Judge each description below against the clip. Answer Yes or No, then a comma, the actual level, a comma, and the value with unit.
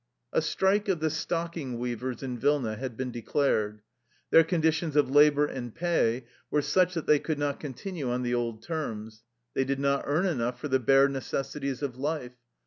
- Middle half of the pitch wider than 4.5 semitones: No, average, 4.2 semitones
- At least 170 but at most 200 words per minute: Yes, average, 185 wpm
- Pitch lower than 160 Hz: Yes, medium, 140 Hz